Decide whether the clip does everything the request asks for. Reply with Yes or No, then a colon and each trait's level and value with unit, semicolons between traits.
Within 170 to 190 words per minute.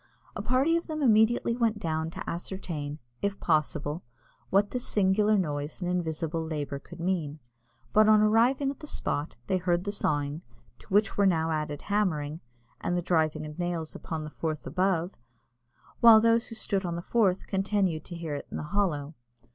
Yes: average, 180 wpm